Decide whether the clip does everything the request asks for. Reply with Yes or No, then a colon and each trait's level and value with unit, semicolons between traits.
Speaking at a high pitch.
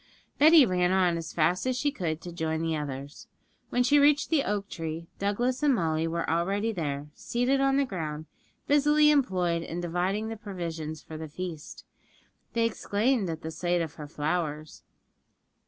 No: medium, 180 Hz